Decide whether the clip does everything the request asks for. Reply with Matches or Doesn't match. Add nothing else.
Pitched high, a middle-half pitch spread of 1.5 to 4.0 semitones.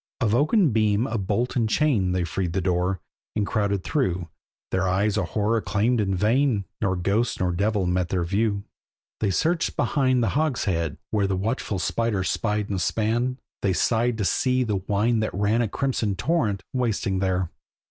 Doesn't match